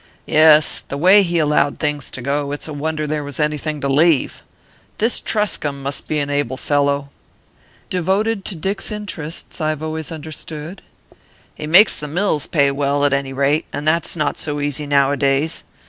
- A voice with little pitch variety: Yes, narrow, 2.2 semitones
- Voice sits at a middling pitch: Yes, medium, 150 Hz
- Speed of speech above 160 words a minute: Yes, average, 170 wpm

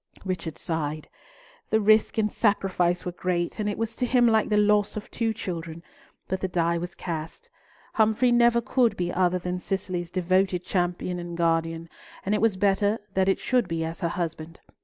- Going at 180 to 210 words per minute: Yes, average, 185 wpm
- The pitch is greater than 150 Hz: Yes, medium, 185 Hz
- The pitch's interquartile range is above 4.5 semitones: No, average, 3.7 semitones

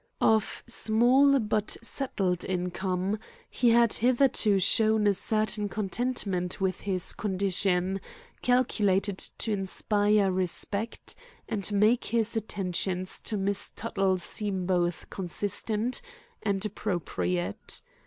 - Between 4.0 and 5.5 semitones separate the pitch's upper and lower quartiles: No, average, 2.8 semitones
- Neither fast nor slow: No, slow, 105 wpm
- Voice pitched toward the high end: Yes, high, 200 Hz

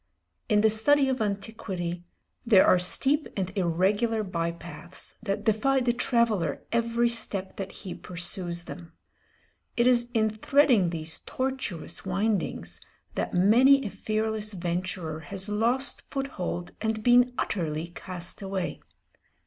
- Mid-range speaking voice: No, high, 205 Hz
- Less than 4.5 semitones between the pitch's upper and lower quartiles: No, average, 4.8 semitones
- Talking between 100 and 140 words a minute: Yes, slow, 135 wpm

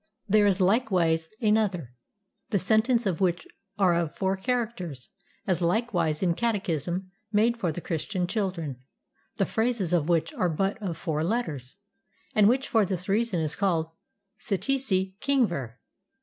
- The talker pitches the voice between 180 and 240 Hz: Yes, high, 190 Hz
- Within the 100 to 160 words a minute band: Yes, average, 150 wpm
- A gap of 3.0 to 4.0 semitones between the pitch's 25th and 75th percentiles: No, average, 4.6 semitones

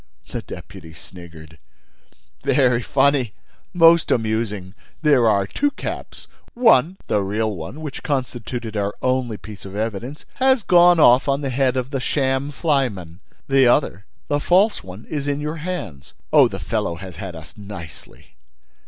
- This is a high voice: No, low, 125 Hz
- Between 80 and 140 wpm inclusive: No, average, 150 wpm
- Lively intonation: Yes, wide, 6.6 semitones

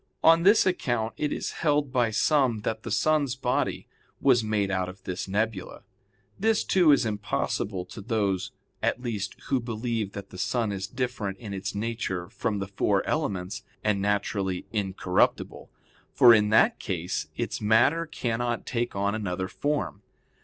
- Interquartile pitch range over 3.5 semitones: Yes, average, 4.0 semitones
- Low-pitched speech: Yes, low, 110 Hz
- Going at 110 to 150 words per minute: No, average, 160 wpm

